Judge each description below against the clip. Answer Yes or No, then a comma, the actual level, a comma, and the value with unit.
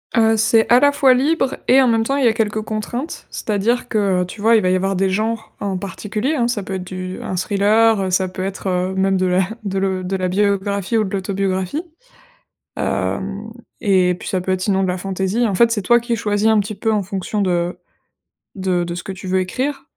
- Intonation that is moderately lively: Yes, average, 3.1 semitones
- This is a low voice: No, high, 200 Hz